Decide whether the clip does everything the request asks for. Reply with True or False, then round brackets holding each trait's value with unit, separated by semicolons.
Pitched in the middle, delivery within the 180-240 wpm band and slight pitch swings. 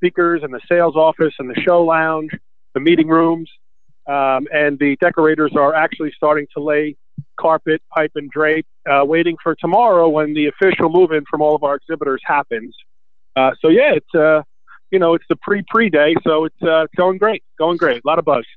True (155 Hz; 200 wpm; 1.9 semitones)